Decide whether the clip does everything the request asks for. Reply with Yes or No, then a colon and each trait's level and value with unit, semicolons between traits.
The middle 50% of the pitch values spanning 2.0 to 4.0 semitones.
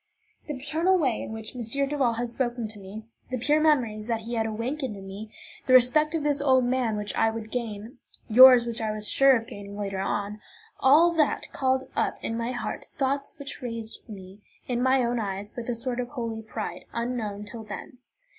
Yes: average, 3.3 semitones